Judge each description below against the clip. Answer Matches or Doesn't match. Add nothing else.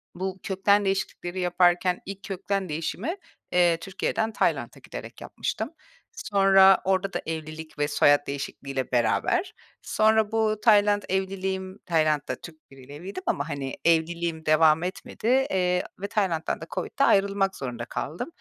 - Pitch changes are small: Doesn't match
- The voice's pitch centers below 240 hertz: Matches